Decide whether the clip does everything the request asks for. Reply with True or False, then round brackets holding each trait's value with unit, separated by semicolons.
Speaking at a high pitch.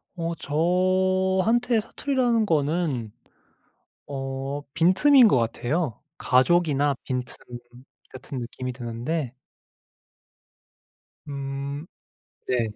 False (150 Hz)